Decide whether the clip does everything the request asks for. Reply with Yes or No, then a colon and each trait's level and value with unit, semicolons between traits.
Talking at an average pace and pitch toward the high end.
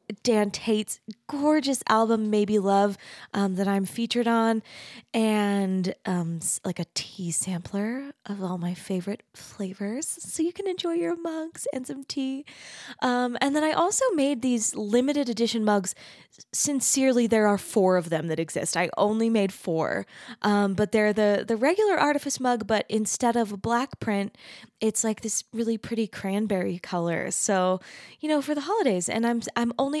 Yes: average, 170 wpm; high, 220 Hz